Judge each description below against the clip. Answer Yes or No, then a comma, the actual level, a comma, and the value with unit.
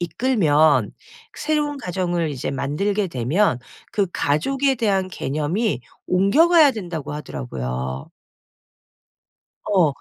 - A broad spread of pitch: Yes, wide, 7.0 semitones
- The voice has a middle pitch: Yes, medium, 175 Hz